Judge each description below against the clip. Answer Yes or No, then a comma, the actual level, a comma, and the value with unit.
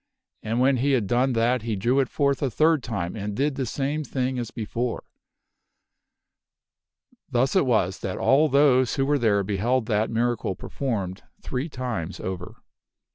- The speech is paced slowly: No, average, 165 wpm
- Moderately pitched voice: No, low, 125 Hz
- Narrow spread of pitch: No, average, 4.0 semitones